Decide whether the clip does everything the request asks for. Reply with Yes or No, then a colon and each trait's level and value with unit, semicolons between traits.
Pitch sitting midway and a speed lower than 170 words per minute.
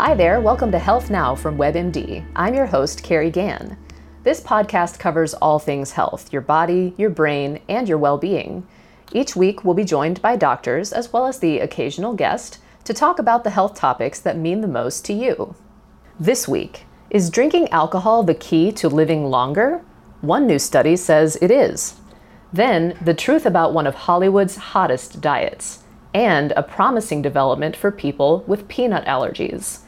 No: medium, 180 Hz; average, 175 wpm